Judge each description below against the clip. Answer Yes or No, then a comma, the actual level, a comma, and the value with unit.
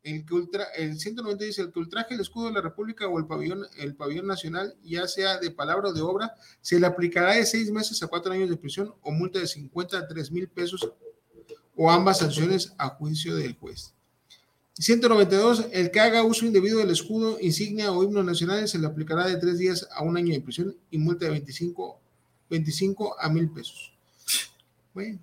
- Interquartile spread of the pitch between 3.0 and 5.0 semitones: Yes, average, 3.6 semitones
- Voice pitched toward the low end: No, medium, 180 Hz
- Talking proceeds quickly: Yes, fast, 195 wpm